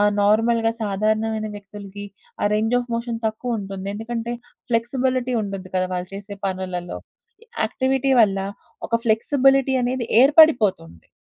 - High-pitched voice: Yes, high, 220 Hz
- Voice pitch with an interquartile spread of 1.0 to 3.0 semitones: No, average, 3.6 semitones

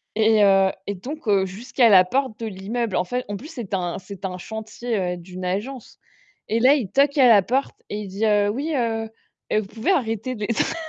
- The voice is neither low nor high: No, high, 220 Hz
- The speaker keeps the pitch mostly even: No, average, 4.1 semitones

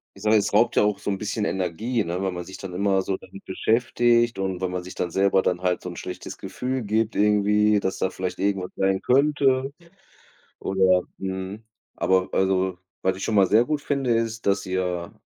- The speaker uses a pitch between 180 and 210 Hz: No, very low, 95 Hz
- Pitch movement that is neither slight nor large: Yes, average, 3.0 semitones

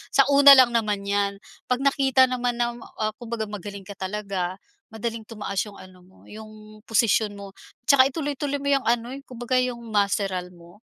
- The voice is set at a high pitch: Yes, high, 220 Hz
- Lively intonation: No, average, 4.0 semitones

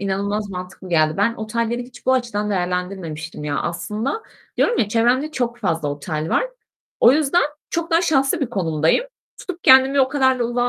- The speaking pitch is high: Yes, high, 225 Hz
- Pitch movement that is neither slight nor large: No, wide, 6.4 semitones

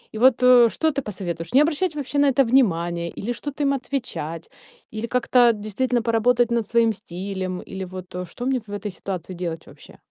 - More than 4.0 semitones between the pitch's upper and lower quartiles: Yes, wide, 5.6 semitones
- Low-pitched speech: No, high, 230 Hz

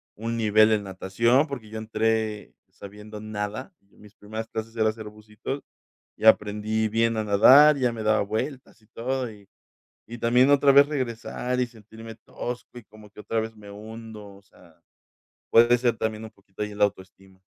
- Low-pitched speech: Yes, low, 110 Hz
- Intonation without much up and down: Yes, narrow, 1.8 semitones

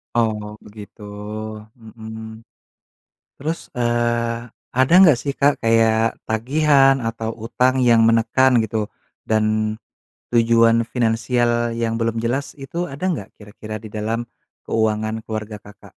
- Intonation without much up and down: Yes, narrow, 2.0 semitones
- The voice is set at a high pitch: No, low, 115 Hz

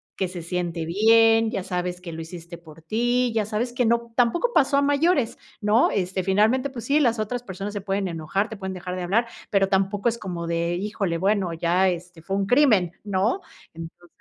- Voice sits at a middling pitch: No, high, 195 Hz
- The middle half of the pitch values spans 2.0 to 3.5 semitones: No, average, 4.5 semitones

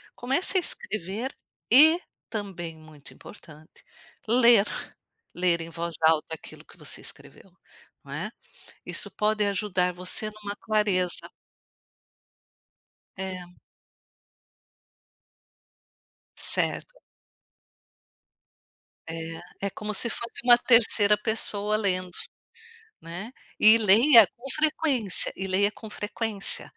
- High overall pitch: Yes, high, 210 Hz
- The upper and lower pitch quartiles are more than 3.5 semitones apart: Yes, average, 4.0 semitones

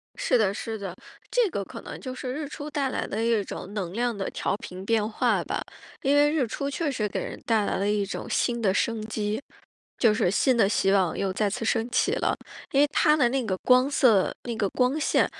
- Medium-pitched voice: No, high, 230 Hz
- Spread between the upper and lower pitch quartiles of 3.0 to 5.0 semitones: Yes, average, 4.7 semitones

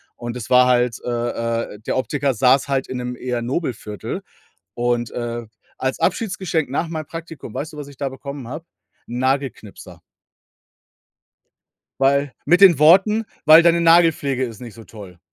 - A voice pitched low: Yes, low, 130 Hz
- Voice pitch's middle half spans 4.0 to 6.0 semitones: Yes, average, 4.5 semitones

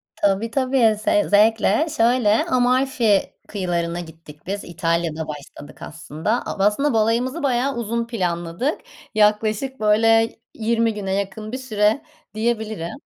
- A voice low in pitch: No, high, 215 Hz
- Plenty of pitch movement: No, average, 3.8 semitones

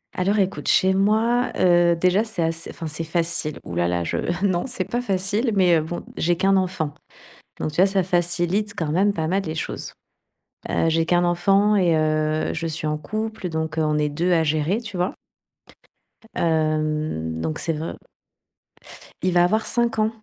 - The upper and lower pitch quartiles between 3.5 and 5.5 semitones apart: Yes, average, 3.8 semitones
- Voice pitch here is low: No, medium, 175 Hz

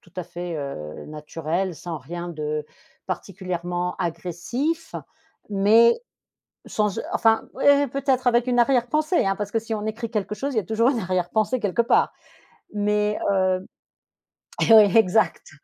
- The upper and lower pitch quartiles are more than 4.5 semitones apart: Yes, average, 4.9 semitones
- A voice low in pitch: No, high, 205 Hz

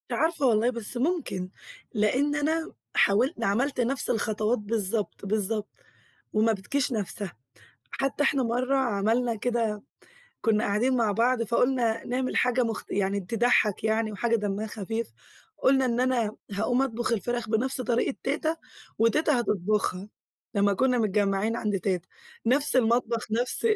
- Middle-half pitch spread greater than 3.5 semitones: No, average, 3.2 semitones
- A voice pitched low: No, high, 230 Hz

